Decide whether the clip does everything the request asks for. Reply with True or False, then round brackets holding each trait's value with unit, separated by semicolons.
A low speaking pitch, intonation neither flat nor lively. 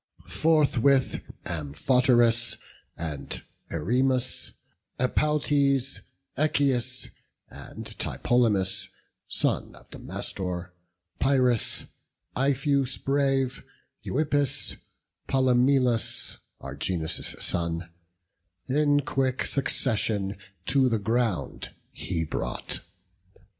False (125 Hz; 5.8 semitones)